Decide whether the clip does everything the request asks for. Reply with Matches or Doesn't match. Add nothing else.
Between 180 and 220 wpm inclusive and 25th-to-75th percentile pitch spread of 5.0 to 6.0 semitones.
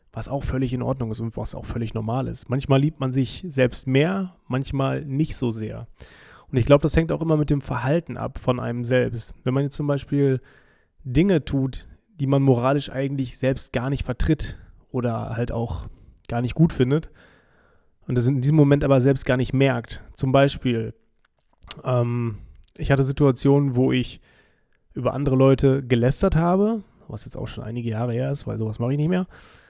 Doesn't match